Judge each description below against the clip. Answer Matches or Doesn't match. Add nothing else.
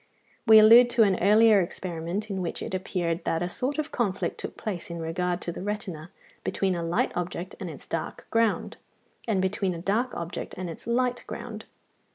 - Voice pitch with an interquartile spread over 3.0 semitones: Matches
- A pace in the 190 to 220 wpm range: Matches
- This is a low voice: Doesn't match